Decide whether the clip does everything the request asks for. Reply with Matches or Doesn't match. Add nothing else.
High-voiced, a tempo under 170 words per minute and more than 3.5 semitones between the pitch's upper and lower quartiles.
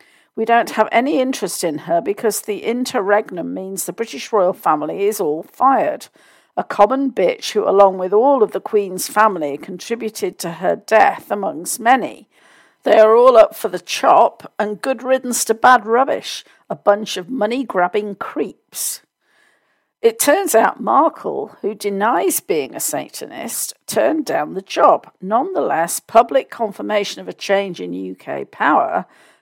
Matches